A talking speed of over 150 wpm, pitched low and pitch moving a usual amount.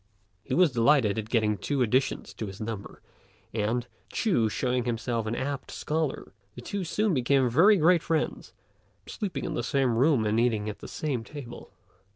Yes: average, 175 wpm; low, 125 Hz; average, 5.0 semitones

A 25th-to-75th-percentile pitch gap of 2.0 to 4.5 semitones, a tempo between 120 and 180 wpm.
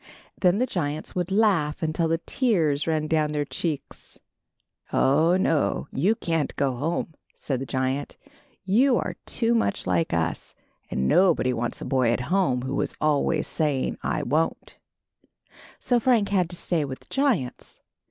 No: average, 5.2 semitones; average, 160 wpm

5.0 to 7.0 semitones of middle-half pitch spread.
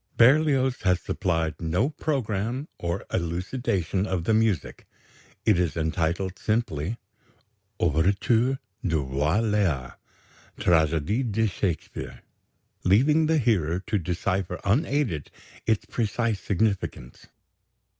Yes: wide, 5.5 semitones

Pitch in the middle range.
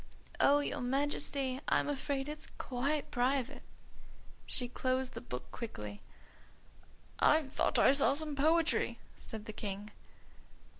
No: very high, 270 Hz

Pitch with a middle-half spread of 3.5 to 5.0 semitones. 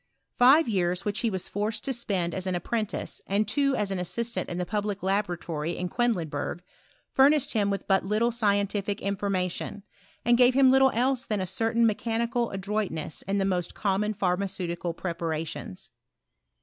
Yes: average, 4.1 semitones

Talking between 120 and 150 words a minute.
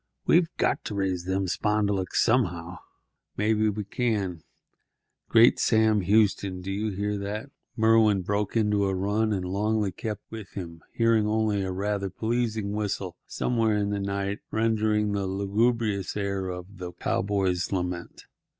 Yes: average, 140 wpm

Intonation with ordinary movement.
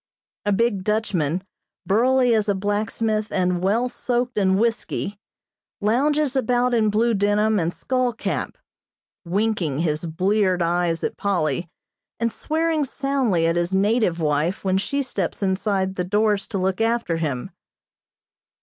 Yes: average, 4.4 semitones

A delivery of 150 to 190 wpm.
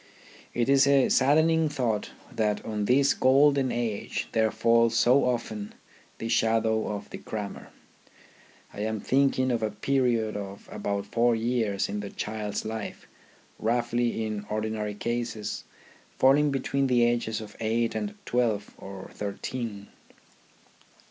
No: slow, 135 wpm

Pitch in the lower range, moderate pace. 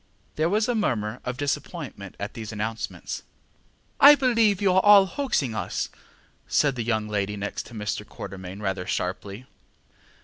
Yes: low, 115 Hz; average, 150 wpm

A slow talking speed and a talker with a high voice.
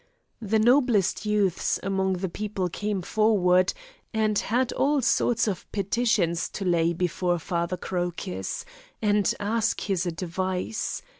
Yes: slow, 125 wpm; high, 195 Hz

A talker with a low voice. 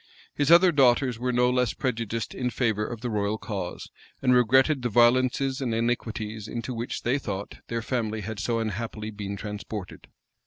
Yes: low, 115 Hz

